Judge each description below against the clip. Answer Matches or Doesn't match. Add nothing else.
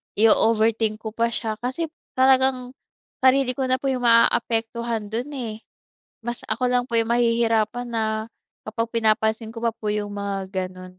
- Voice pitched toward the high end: Matches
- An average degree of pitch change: Doesn't match